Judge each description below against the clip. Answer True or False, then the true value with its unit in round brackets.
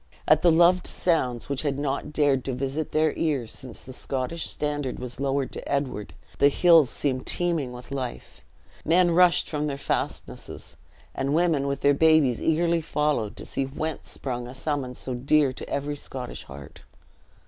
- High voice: False (140 Hz)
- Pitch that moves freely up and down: False (3.3 semitones)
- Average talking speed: True (170 wpm)